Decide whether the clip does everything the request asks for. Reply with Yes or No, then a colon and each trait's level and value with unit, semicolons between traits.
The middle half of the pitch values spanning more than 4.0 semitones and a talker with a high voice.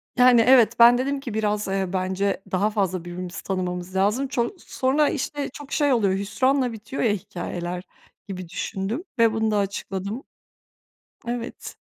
Yes: average, 4.8 semitones; high, 210 Hz